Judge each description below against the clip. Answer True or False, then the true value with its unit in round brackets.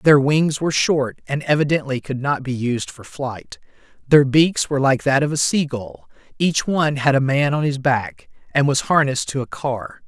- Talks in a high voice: False (140 Hz)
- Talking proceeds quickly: True (210 wpm)